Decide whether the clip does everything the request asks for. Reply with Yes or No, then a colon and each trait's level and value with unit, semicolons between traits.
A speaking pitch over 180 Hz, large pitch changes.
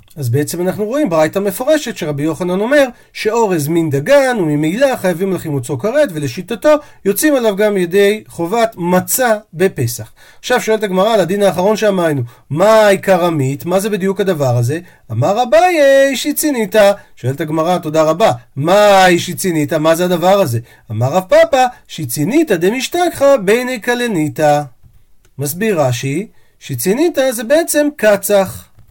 Yes: high, 190 Hz; wide, 7.0 semitones